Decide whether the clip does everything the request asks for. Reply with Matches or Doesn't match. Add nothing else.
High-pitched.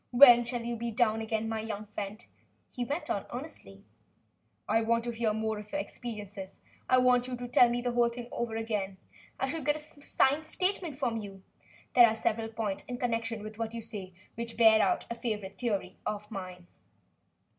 Matches